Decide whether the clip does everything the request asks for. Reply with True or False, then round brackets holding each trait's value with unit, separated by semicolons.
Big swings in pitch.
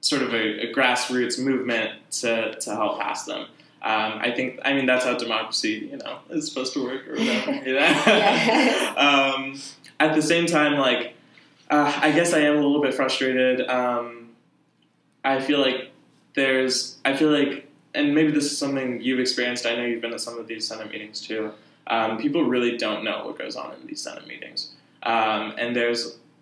False (3.7 semitones)